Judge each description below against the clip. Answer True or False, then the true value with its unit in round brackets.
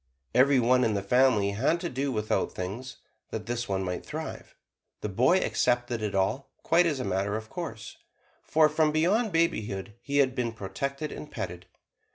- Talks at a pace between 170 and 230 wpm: True (175 wpm)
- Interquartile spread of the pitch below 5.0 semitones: False (5.4 semitones)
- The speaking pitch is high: False (120 Hz)